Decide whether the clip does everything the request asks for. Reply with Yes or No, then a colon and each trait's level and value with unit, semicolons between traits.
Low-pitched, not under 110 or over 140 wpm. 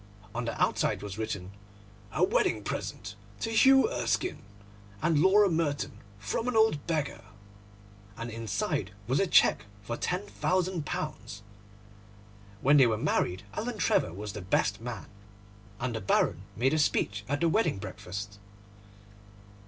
Yes: low, 120 Hz; slow, 135 wpm